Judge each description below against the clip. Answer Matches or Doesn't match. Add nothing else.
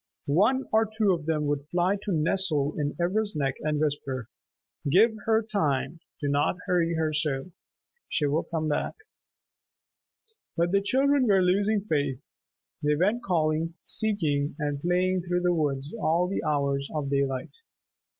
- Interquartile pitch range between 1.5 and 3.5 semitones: Doesn't match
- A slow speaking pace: Doesn't match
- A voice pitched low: Doesn't match